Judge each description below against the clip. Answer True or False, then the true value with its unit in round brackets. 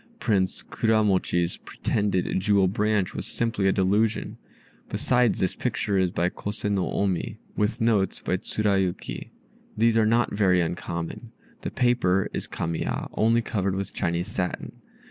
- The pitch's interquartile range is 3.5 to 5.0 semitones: False (3.0 semitones)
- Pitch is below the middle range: True (100 Hz)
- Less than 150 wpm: True (140 wpm)